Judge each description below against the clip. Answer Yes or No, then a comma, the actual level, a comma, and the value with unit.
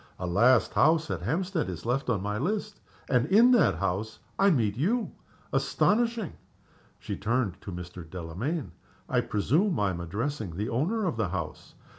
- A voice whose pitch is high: No, low, 120 Hz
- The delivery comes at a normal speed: Yes, average, 165 wpm